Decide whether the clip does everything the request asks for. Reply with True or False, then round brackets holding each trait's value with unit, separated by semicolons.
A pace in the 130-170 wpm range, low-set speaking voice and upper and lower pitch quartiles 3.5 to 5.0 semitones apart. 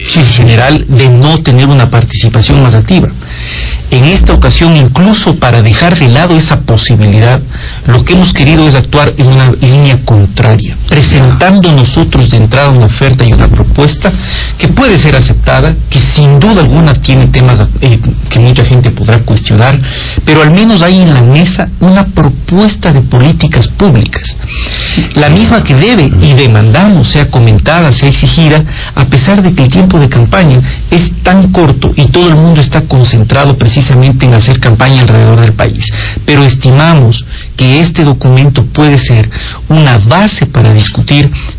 True (160 wpm; 130 Hz; 4.6 semitones)